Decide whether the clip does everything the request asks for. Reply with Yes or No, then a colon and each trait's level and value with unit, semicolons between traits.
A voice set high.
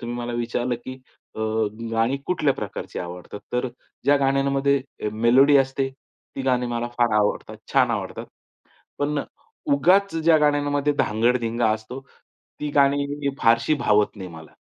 No: low, 130 Hz